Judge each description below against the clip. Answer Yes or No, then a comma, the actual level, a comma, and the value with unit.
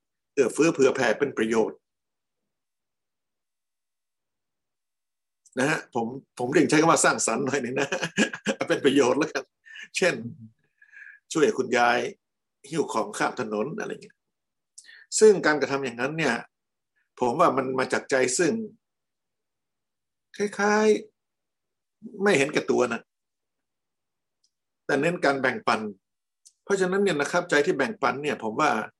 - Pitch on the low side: No, high, 200 Hz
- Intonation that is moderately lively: No, wide, 7.8 semitones